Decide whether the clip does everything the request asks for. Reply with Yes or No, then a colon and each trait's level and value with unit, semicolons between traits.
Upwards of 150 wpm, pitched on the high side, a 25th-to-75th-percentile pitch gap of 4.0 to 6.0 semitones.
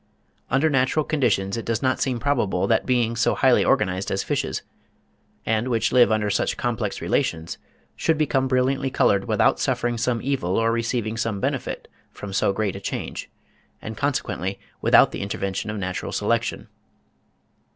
No: average, 160 wpm; low, 115 Hz; average, 4.3 semitones